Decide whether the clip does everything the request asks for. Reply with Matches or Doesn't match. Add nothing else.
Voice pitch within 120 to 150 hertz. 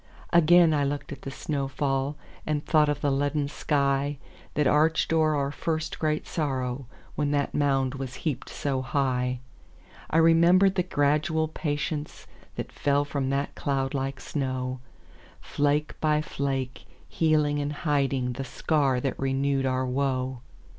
Matches